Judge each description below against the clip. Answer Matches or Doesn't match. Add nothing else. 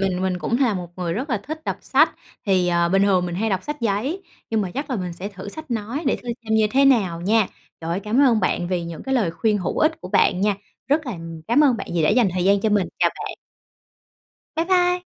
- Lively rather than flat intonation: Matches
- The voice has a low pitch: Doesn't match